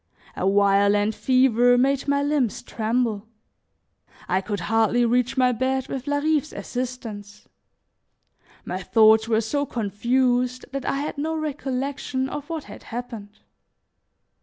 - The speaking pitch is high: Yes, high, 245 Hz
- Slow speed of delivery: Yes, slow, 125 wpm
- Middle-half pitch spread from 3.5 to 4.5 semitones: Yes, average, 3.8 semitones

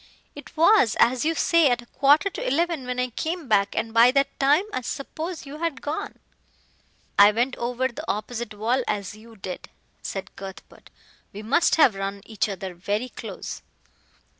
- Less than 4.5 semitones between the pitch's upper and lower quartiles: No, wide, 5.5 semitones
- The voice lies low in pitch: No, high, 245 Hz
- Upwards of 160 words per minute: Yes, average, 175 wpm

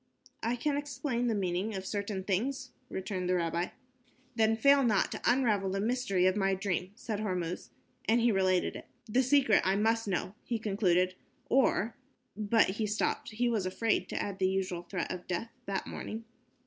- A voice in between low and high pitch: No, high, 210 Hz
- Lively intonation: No, average, 3.8 semitones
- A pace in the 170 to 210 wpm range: Yes, average, 185 wpm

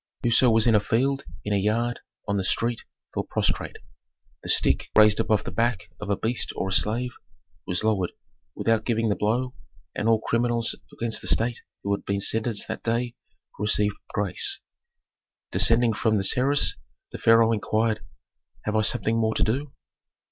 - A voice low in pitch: Yes, low, 110 Hz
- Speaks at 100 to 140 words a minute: No, average, 170 wpm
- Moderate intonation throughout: No, narrow, 2.1 semitones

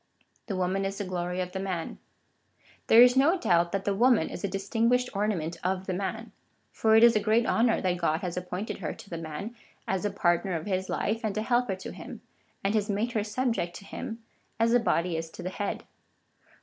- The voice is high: Yes, high, 195 Hz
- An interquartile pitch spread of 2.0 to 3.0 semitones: No, average, 3.8 semitones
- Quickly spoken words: Yes, fast, 220 wpm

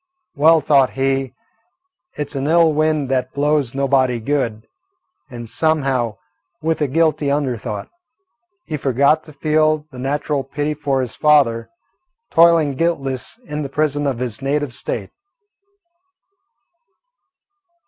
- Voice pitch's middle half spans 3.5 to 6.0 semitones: No, average, 2.7 semitones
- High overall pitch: No, medium, 140 Hz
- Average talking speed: No, slow, 130 wpm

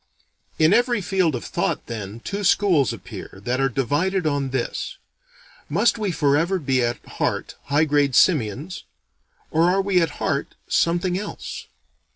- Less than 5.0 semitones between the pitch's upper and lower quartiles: No, wide, 5.6 semitones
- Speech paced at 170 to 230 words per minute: No, average, 150 wpm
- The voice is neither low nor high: Yes, medium, 155 Hz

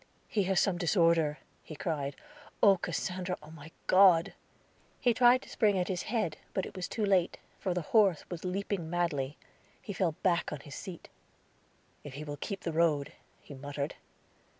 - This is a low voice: No, medium, 175 Hz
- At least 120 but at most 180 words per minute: Yes, average, 170 wpm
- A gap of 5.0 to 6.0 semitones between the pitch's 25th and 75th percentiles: No, average, 4.0 semitones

